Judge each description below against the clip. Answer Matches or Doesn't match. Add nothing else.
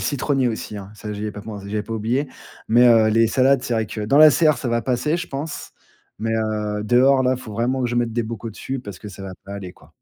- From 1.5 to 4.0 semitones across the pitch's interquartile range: Matches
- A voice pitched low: Matches